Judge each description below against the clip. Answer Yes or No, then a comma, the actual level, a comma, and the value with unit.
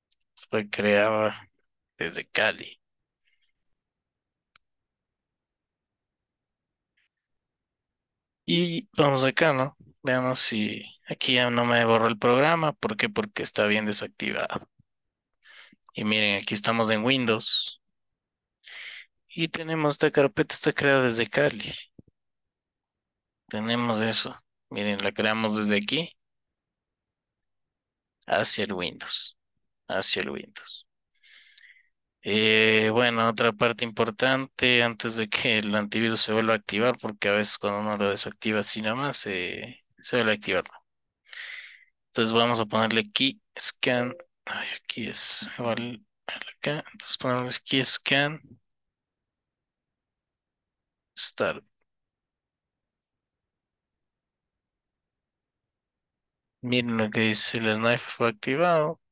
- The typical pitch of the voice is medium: No, low, 115 Hz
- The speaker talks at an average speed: No, slow, 105 wpm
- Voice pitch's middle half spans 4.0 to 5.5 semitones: No, average, 3.2 semitones